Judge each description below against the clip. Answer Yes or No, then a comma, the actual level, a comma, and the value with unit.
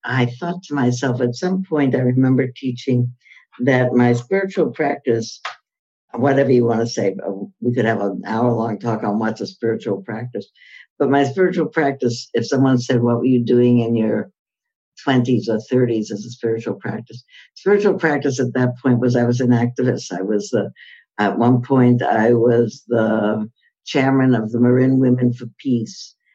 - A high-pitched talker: No, low, 125 Hz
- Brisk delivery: No, average, 175 wpm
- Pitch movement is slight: Yes, narrow, 2.3 semitones